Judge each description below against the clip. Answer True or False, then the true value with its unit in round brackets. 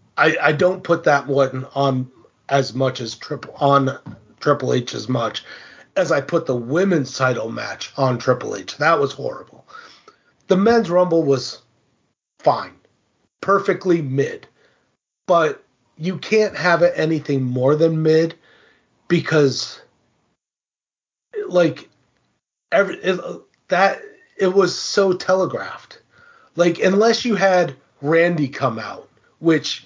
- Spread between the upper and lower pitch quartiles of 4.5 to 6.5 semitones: True (5.1 semitones)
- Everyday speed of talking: False (125 wpm)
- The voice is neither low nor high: True (160 Hz)